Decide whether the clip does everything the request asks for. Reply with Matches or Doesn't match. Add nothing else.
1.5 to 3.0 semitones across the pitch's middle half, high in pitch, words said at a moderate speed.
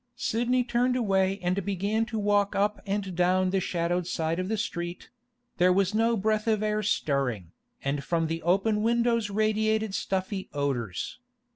Doesn't match